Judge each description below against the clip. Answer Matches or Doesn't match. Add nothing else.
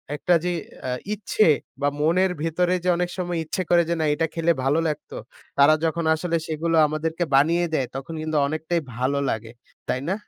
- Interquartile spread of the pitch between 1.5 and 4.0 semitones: Matches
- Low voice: Doesn't match